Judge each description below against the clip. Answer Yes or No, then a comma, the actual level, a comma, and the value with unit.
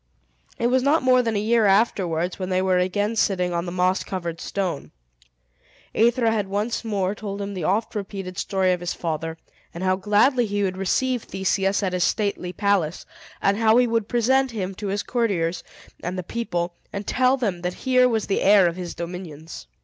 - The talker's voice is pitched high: Yes, high, 195 Hz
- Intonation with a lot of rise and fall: No, average, 3.7 semitones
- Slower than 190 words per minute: No, average, 195 wpm